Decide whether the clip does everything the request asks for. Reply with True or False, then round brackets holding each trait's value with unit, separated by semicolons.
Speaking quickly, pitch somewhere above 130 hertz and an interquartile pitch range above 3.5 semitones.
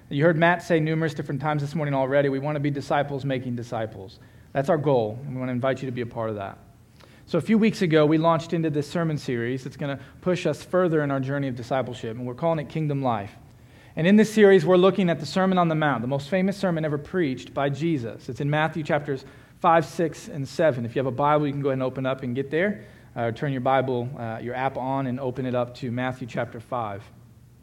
True (260 wpm; 140 Hz; 4.3 semitones)